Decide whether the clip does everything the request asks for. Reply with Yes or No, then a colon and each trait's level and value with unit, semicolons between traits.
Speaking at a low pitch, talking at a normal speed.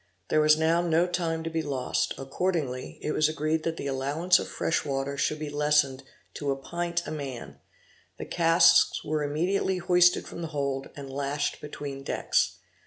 No: medium, 150 Hz; average, 175 wpm